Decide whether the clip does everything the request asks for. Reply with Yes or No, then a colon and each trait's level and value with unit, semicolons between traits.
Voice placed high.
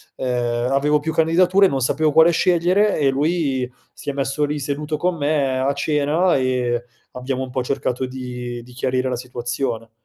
No: low, 135 Hz